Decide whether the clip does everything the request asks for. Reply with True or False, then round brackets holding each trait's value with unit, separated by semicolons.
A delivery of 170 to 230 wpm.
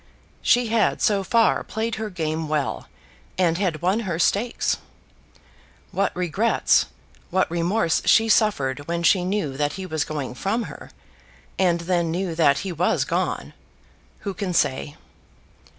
False (145 wpm)